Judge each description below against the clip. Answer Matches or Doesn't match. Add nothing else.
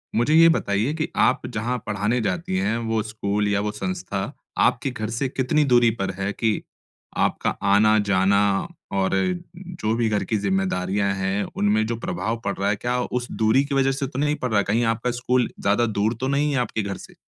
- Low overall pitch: Matches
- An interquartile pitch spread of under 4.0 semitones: Doesn't match